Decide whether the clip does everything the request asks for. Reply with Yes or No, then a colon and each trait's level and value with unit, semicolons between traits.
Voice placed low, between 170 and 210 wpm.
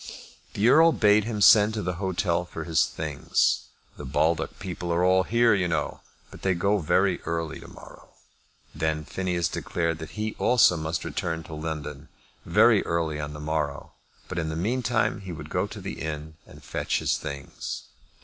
Yes: very low, 85 Hz; average, 180 wpm